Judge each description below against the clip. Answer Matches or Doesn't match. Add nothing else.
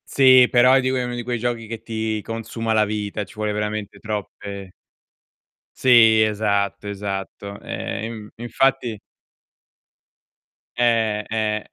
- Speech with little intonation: Matches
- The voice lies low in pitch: Matches